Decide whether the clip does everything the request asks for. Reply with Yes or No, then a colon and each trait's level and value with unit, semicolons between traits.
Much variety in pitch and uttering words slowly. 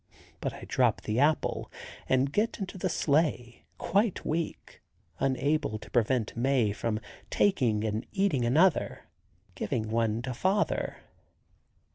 Yes: wide, 6.4 semitones; slow, 125 wpm